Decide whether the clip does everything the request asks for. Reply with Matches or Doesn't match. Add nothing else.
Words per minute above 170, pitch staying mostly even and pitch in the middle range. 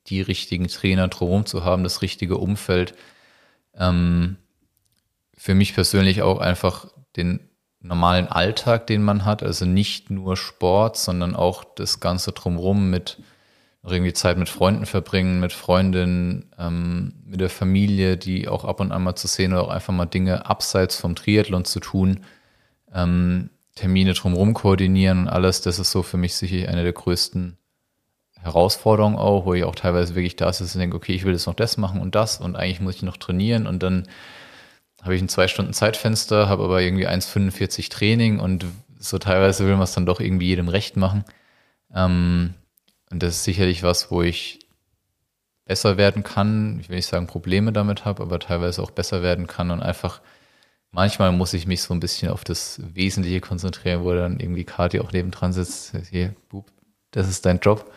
Doesn't match